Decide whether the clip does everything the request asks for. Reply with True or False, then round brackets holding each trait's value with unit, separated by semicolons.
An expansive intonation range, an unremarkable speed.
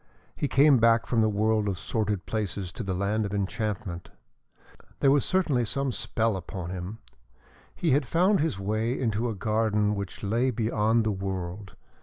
False (3.0 semitones; 170 wpm)